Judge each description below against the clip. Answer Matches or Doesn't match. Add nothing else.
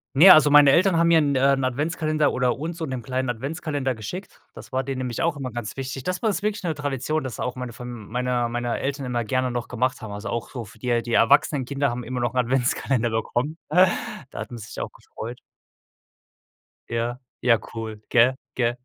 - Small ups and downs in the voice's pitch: Doesn't match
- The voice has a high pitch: Doesn't match